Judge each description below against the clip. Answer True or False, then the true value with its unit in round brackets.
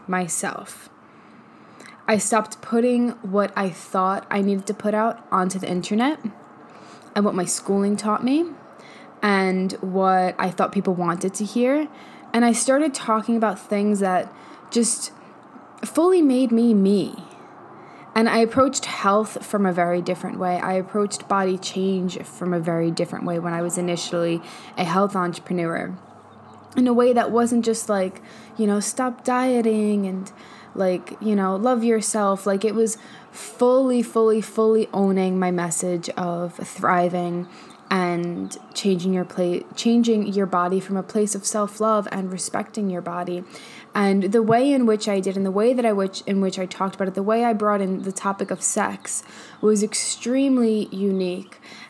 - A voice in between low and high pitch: False (200 Hz)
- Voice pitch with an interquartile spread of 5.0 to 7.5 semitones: False (3.3 semitones)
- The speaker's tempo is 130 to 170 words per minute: True (165 wpm)